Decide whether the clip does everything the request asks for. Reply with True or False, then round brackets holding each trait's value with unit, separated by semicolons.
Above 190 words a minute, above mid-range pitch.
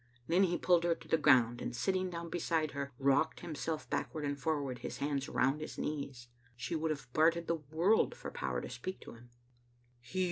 False (200 wpm; 155 Hz)